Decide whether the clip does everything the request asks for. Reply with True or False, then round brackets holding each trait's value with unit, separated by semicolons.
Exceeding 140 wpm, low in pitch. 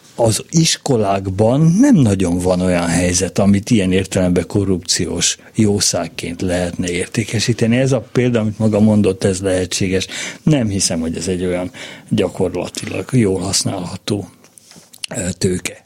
False (120 wpm; 100 Hz)